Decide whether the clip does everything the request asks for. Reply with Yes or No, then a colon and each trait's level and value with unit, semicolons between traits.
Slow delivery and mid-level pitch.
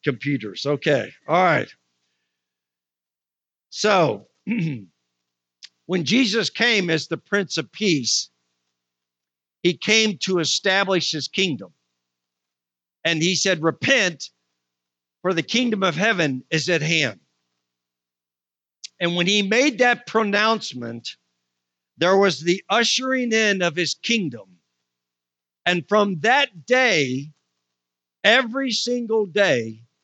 Yes: slow, 105 wpm; medium, 145 Hz